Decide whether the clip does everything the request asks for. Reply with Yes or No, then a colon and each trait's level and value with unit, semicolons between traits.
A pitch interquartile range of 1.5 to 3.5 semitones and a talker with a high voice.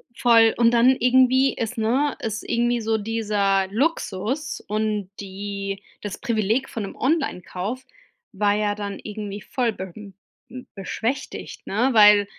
Yes: average, 3.0 semitones; high, 220 Hz